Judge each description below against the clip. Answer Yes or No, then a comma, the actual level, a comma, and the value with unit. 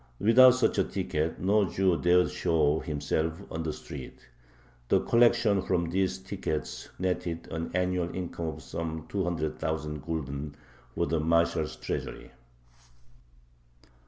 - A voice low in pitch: Yes, very low, 85 Hz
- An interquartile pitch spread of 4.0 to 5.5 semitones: No, average, 3.0 semitones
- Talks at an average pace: No, slow, 125 wpm